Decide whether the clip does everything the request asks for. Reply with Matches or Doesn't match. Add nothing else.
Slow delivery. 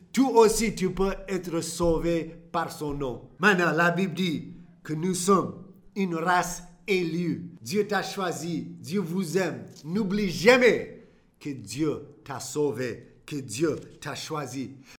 Matches